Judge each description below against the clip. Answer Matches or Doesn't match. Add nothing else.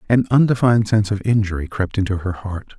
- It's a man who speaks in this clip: Matches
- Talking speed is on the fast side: Doesn't match